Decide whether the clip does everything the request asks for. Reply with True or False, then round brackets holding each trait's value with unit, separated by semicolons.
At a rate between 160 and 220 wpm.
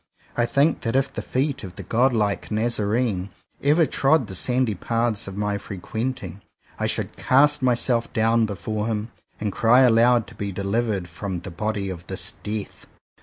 True (170 wpm)